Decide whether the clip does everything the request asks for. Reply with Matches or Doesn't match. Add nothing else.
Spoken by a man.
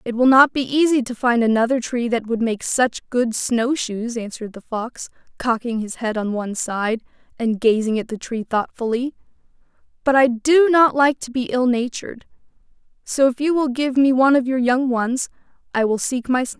Doesn't match